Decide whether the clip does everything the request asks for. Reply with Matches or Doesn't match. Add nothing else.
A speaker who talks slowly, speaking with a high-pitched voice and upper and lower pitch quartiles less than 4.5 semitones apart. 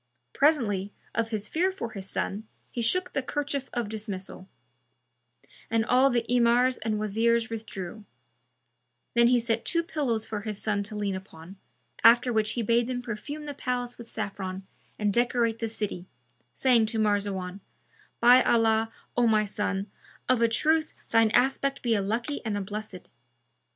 Doesn't match